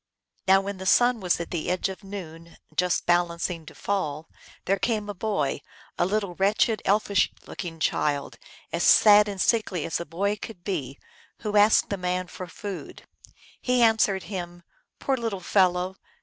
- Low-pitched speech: No, high, 190 Hz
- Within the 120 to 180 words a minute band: Yes, average, 170 wpm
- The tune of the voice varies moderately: Yes, average, 3.0 semitones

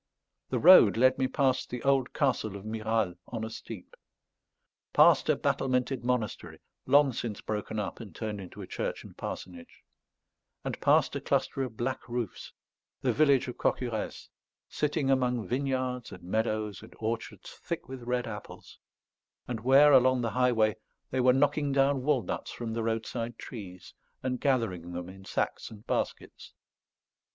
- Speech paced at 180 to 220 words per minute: No, average, 155 wpm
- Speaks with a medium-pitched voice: No, low, 120 Hz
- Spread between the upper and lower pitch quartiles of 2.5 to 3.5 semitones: Yes, average, 3.2 semitones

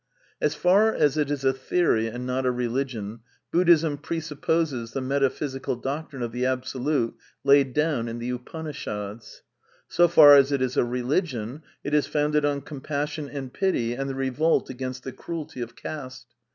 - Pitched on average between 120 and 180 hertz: Yes, low, 135 Hz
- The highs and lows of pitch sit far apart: No, average, 3.1 semitones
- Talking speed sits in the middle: Yes, average, 165 wpm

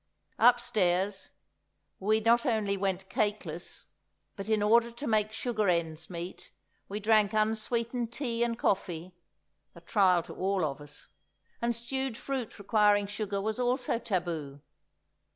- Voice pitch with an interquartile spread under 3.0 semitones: No, average, 3.5 semitones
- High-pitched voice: Yes, high, 210 Hz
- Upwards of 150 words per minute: No, slow, 135 wpm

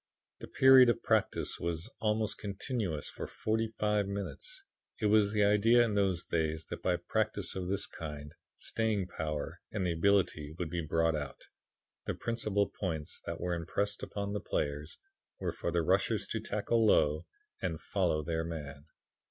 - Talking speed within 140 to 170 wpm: Yes, average, 160 wpm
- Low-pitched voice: Yes, very low, 95 Hz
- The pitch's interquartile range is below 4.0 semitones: No, average, 4.6 semitones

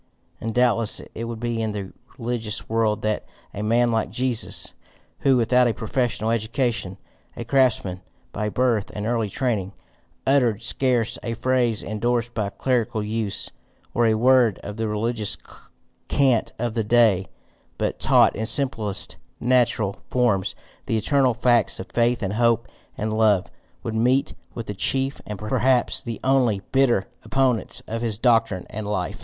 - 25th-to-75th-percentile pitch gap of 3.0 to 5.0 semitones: No, narrow, 2.4 semitones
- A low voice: Yes, low, 115 Hz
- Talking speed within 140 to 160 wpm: Yes, average, 155 wpm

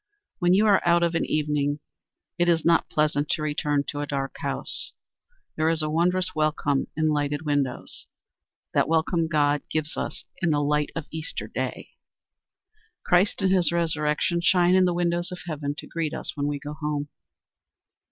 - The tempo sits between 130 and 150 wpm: No, average, 175 wpm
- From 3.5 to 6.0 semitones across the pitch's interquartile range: No, average, 2.7 semitones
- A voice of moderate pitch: Yes, medium, 155 Hz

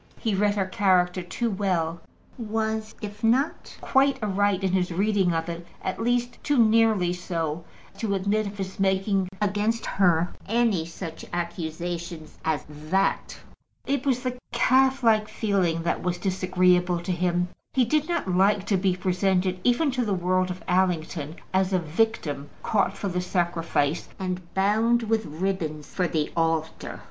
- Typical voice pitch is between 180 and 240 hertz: Yes, high, 190 Hz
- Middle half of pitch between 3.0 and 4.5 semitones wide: Yes, average, 3.7 semitones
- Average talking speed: Yes, average, 155 wpm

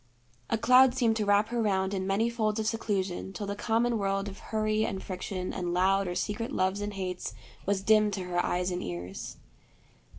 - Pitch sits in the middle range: No, high, 200 Hz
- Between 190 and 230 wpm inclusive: Yes, average, 200 wpm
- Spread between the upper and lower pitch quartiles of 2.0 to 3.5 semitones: Yes, narrow, 2.6 semitones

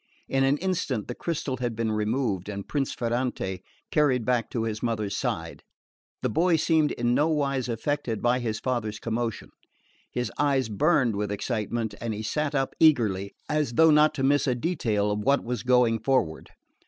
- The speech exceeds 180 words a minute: No, average, 175 wpm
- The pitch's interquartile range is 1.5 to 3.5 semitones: No, average, 4.6 semitones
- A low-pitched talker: Yes, low, 120 Hz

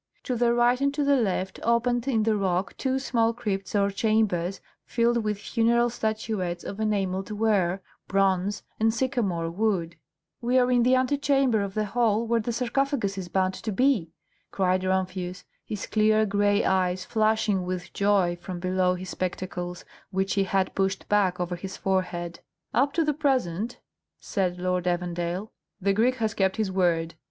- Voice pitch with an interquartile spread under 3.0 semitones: No, average, 4.1 semitones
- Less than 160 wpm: No, average, 165 wpm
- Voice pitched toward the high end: Yes, high, 200 Hz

